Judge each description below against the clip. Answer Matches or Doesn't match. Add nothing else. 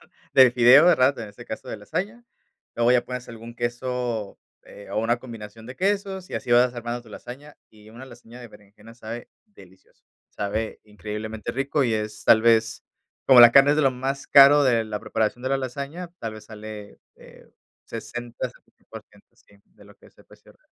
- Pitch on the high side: Doesn't match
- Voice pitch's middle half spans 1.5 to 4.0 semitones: Matches